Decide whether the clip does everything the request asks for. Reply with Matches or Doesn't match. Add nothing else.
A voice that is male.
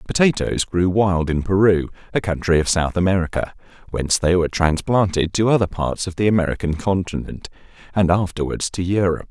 Matches